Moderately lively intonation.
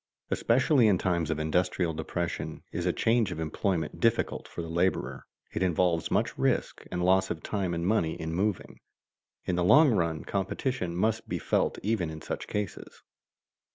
Yes: average, 4.0 semitones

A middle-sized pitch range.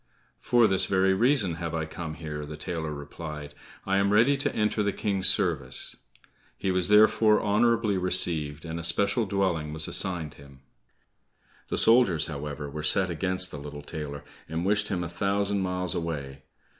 Yes: average, 4.7 semitones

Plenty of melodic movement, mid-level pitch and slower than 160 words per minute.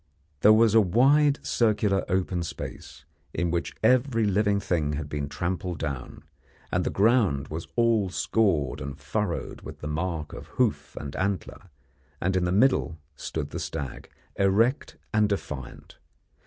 No: wide, 5.9 semitones; very low, 95 Hz; average, 150 wpm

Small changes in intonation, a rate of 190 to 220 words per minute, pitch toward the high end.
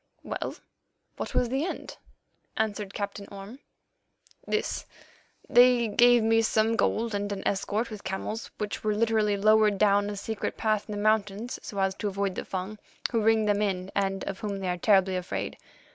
No: narrow, 1.9 semitones; average, 180 wpm; high, 210 Hz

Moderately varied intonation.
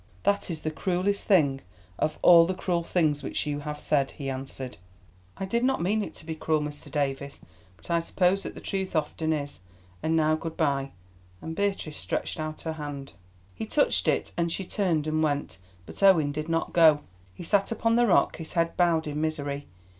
Yes: average, 3.4 semitones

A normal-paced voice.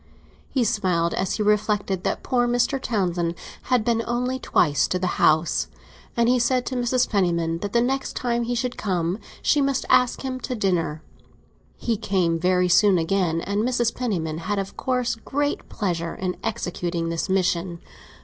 Yes: average, 170 wpm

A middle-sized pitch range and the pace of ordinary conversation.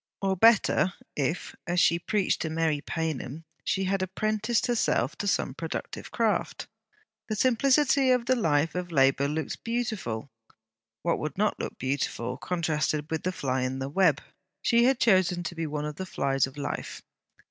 No: wide, 6.5 semitones; average, 170 wpm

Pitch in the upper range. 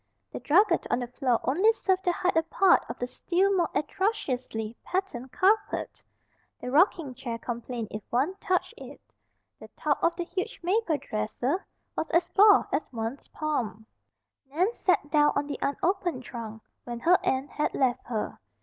Yes: very high, 295 Hz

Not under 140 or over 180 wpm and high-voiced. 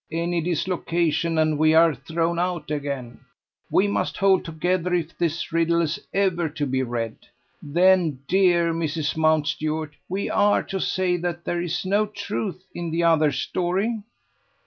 No: average, 150 wpm; medium, 170 Hz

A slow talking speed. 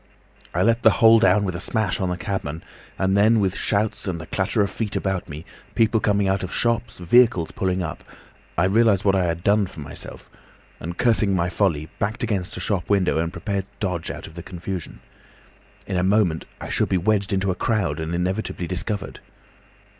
No: fast, 205 wpm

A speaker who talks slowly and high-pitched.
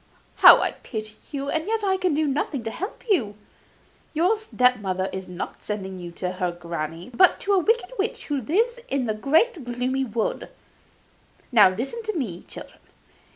No: average, 180 wpm; very high, 255 Hz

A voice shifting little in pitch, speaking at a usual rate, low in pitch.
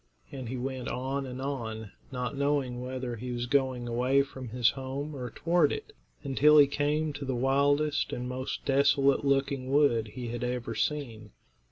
Yes: narrow, 2.3 semitones; average, 175 wpm; low, 130 Hz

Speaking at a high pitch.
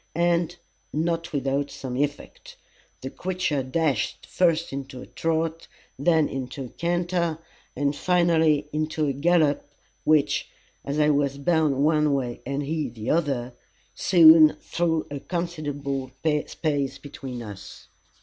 No: medium, 150 Hz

